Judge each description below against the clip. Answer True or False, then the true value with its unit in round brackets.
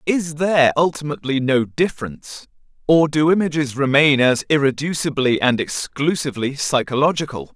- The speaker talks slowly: True (110 wpm)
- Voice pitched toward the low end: False (145 Hz)